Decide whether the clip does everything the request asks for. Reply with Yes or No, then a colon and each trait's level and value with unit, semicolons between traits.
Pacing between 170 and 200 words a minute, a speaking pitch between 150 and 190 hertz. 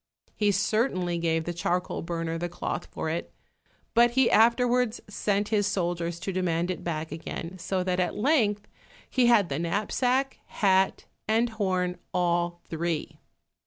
No: average, 150 wpm; medium, 185 Hz